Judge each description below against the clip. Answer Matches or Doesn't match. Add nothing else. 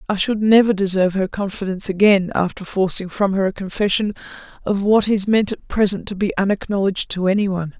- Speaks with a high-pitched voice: Matches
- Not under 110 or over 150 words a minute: Doesn't match